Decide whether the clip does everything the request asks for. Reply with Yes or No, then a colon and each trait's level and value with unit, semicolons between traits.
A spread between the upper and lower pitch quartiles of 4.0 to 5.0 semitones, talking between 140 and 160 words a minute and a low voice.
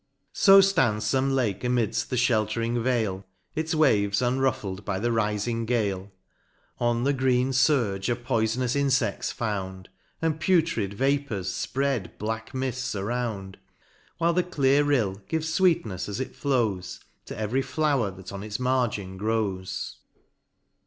Yes: average, 4.5 semitones; average, 150 wpm; low, 120 Hz